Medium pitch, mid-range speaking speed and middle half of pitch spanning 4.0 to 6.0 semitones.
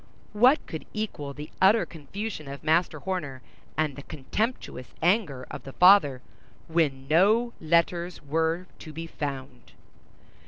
No: medium, 160 Hz; slow, 130 wpm; average, 5.0 semitones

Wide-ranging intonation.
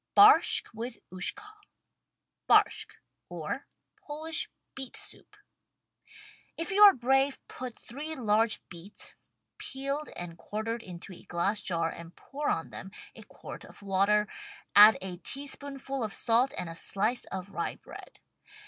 Yes: wide, 6.3 semitones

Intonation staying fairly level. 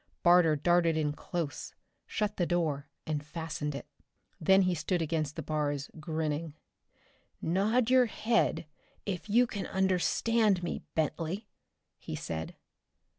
No: average, 3.9 semitones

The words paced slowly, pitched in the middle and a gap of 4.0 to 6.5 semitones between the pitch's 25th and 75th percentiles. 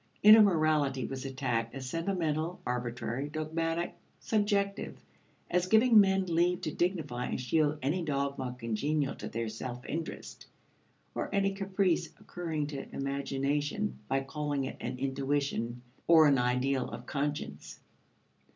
Yes: slow, 130 wpm; medium, 145 Hz; average, 4.5 semitones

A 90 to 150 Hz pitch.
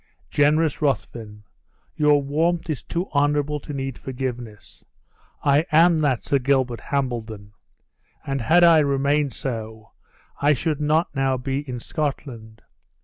Yes: medium, 140 Hz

